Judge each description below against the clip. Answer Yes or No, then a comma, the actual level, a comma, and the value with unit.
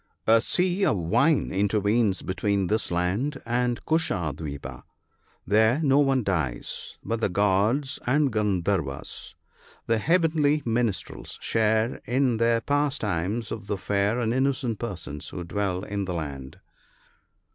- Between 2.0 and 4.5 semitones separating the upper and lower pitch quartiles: No, wide, 5.4 semitones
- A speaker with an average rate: No, slow, 130 wpm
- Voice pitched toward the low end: Yes, low, 110 Hz